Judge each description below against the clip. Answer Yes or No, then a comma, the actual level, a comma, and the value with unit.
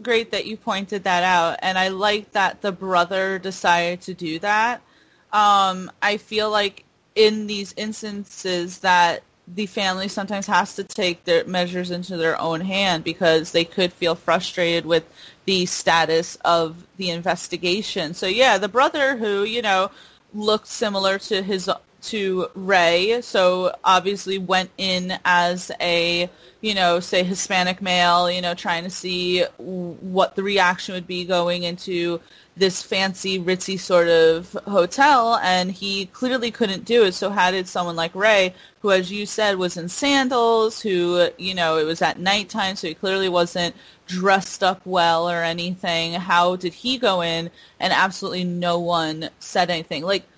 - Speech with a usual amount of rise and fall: No, narrow, 2.3 semitones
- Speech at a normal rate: Yes, average, 160 wpm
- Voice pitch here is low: No, medium, 185 Hz